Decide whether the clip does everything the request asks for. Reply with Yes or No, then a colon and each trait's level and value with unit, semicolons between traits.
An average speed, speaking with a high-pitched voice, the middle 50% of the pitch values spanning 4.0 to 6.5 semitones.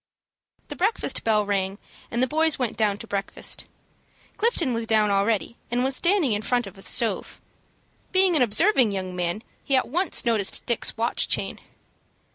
Yes: average, 165 wpm; high, 230 Hz; average, 5.1 semitones